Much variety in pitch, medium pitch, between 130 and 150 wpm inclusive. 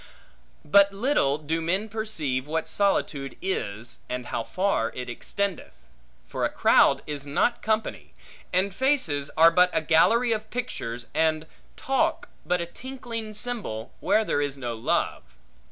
Yes: wide, 7.5 semitones; medium, 175 Hz; average, 145 wpm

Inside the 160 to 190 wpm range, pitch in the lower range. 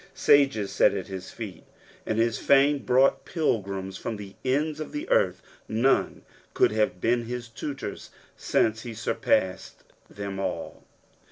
No: average, 145 wpm; low, 115 Hz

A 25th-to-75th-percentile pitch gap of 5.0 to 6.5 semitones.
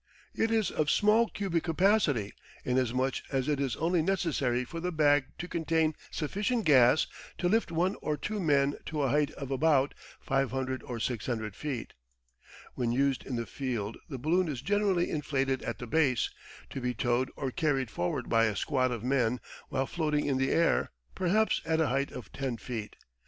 No: average, 4.5 semitones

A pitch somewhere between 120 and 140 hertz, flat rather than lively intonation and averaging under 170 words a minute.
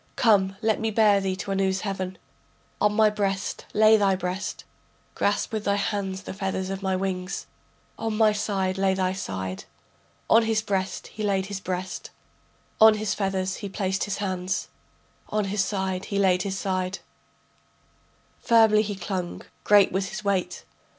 No: high, 195 Hz; narrow, 1.8 semitones; average, 160 wpm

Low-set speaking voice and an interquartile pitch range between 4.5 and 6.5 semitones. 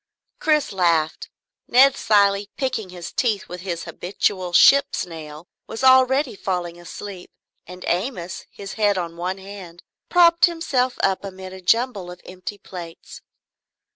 No: high, 190 Hz; wide, 5.5 semitones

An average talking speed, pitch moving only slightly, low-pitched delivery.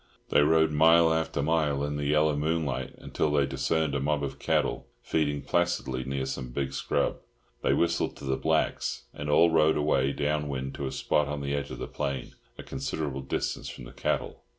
Yes: average, 195 wpm; narrow, 2.3 semitones; very low, 75 Hz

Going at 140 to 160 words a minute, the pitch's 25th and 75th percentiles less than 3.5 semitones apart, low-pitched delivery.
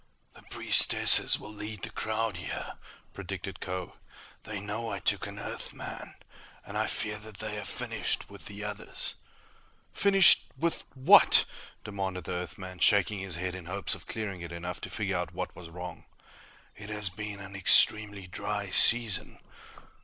Yes: average, 155 wpm; narrow, 2.5 semitones; low, 100 Hz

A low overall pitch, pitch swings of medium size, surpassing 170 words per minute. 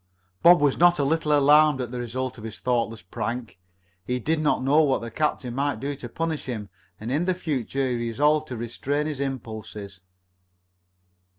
Yes: low, 130 Hz; average, 4.2 semitones; average, 185 wpm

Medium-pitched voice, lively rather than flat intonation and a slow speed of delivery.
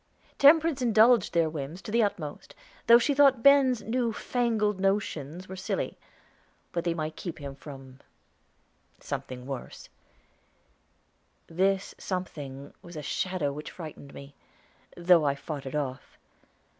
Yes: medium, 175 Hz; wide, 7.6 semitones; slow, 130 wpm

